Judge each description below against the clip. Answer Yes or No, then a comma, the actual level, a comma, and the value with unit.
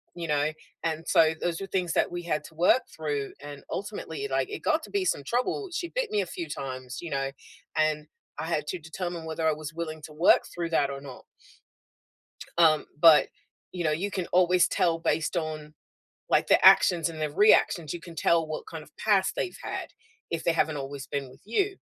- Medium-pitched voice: Yes, medium, 165 Hz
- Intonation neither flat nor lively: Yes, average, 3.2 semitones